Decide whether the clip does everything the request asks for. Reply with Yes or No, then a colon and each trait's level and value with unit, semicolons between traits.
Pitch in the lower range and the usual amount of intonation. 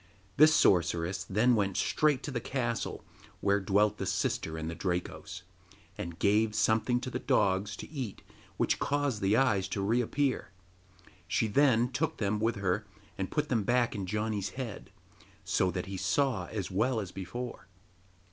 Yes: low, 105 Hz; average, 4.3 semitones